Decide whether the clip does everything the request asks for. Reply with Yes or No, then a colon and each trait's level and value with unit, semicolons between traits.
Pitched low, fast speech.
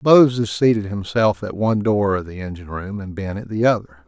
Yes: low, 105 Hz; fast, 220 wpm